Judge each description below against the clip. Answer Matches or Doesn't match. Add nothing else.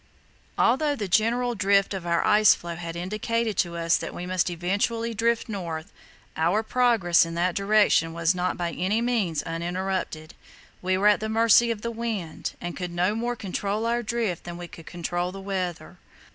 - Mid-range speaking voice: Doesn't match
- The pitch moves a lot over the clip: Doesn't match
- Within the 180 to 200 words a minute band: Matches